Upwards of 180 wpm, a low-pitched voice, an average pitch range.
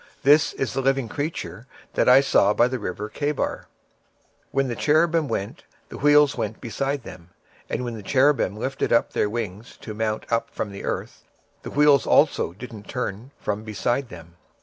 Yes: average, 195 wpm; low, 120 Hz; average, 4.7 semitones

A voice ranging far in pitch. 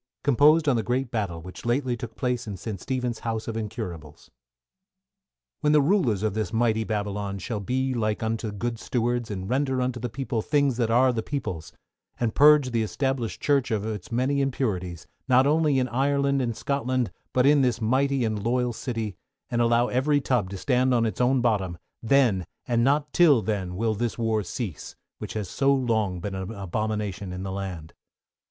No: average, 3.7 semitones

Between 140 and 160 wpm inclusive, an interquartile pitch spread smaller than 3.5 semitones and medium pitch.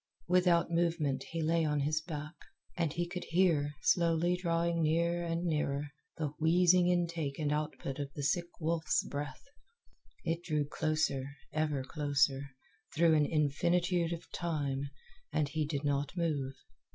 Yes: average, 145 wpm; average, 2.7 semitones; medium, 160 Hz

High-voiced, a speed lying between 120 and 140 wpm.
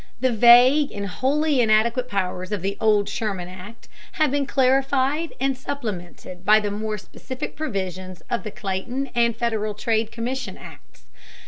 No: high, 225 Hz; average, 150 wpm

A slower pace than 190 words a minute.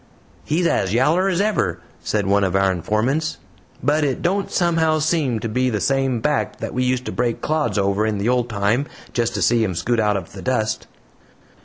No: fast, 205 wpm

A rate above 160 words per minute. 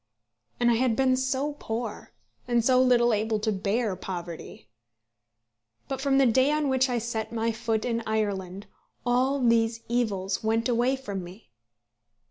No: average, 155 wpm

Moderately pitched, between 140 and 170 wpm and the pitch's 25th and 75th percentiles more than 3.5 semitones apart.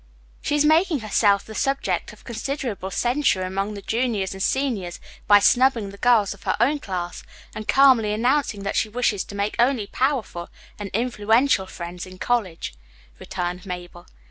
No: high, 215 Hz; average, 165 wpm; average, 4.8 semitones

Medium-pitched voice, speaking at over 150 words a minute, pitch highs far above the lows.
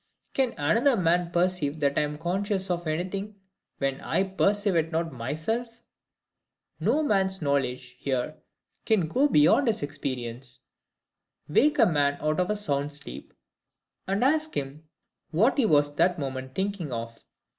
No: medium, 165 Hz; average, 145 wpm; wide, 6.0 semitones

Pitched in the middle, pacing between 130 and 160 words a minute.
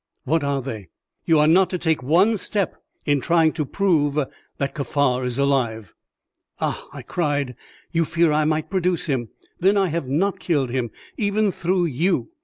No: medium, 155 Hz; average, 175 wpm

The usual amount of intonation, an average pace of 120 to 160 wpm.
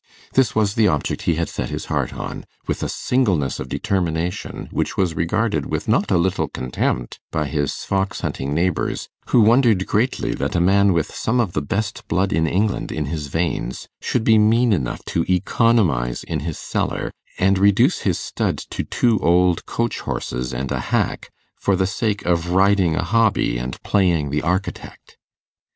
No: average, 4.9 semitones; average, 180 wpm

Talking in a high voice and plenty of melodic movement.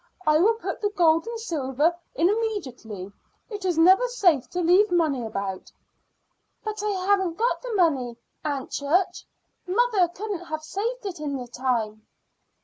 Yes: very high, 345 Hz; wide, 7.0 semitones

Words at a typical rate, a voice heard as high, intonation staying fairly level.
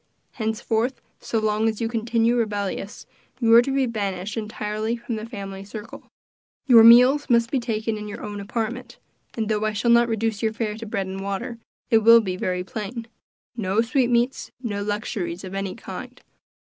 Yes: average, 180 wpm; high, 220 Hz; narrow, 2.3 semitones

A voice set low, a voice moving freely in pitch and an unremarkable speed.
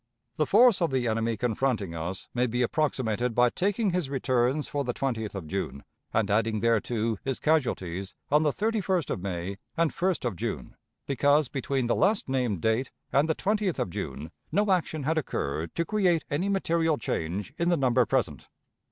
Yes: low, 130 Hz; wide, 6.7 semitones; average, 180 wpm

